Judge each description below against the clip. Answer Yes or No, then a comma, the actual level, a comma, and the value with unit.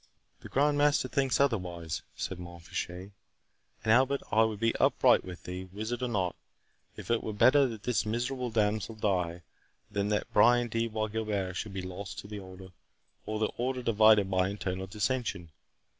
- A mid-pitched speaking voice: No, low, 105 Hz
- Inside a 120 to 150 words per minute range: No, average, 170 wpm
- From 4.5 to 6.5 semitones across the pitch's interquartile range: No, average, 4.1 semitones